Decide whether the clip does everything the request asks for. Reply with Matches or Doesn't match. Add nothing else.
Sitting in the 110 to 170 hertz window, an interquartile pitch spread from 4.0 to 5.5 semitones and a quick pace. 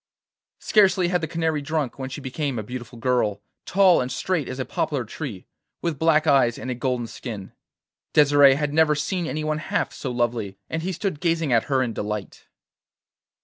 Doesn't match